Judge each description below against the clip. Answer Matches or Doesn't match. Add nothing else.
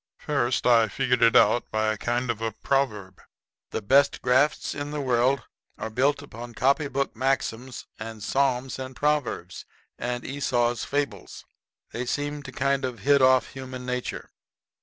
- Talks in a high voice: Doesn't match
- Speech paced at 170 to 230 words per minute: Doesn't match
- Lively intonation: Doesn't match